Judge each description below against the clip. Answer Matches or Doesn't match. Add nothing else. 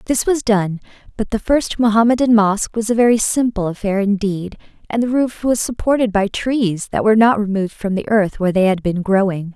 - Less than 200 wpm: Doesn't match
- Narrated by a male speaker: Doesn't match